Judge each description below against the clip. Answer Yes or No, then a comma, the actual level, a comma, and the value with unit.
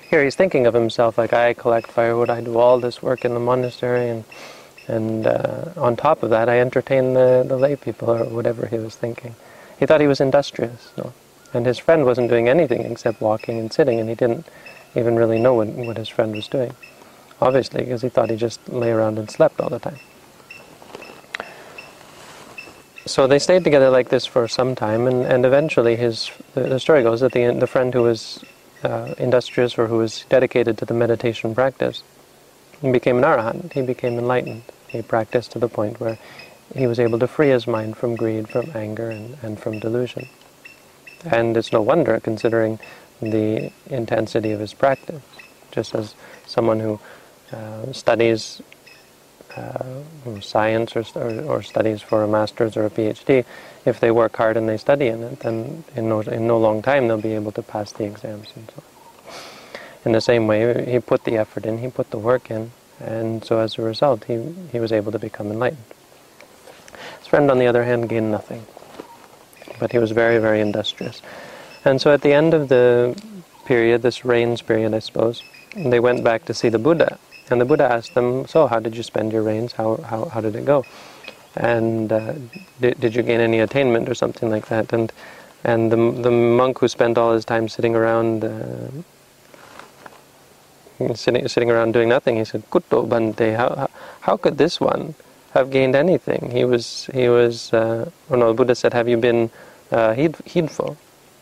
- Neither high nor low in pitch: No, low, 115 Hz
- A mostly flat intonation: Yes, narrow, 1.9 semitones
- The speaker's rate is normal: Yes, average, 195 wpm